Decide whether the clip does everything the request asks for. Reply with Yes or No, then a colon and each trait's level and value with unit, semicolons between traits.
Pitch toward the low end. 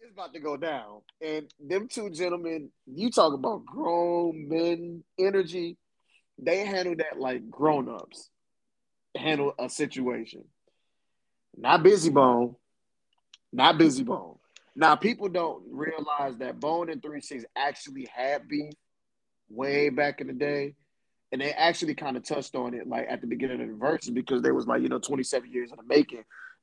No: medium, 155 Hz